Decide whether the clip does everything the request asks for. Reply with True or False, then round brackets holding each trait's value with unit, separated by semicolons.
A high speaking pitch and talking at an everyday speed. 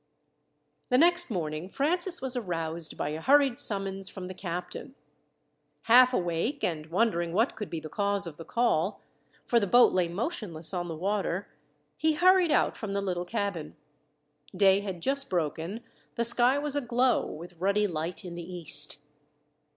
True (195 Hz; 165 wpm)